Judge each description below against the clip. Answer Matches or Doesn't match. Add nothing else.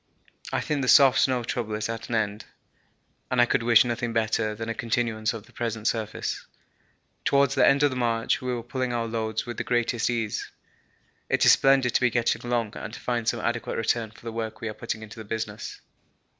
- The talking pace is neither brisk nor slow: Doesn't match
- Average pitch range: Doesn't match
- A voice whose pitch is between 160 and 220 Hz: Doesn't match